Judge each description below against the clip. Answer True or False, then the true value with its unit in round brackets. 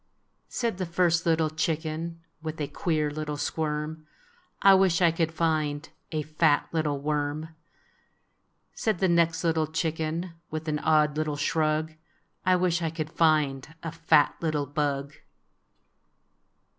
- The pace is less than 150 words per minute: True (140 wpm)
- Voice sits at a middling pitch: True (155 Hz)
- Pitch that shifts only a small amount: True (1.6 semitones)